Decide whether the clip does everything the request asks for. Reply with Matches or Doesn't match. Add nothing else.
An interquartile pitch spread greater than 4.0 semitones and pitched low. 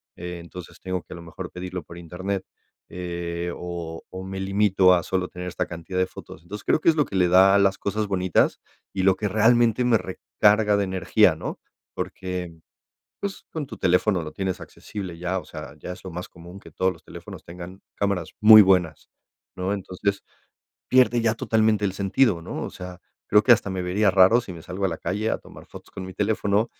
Doesn't match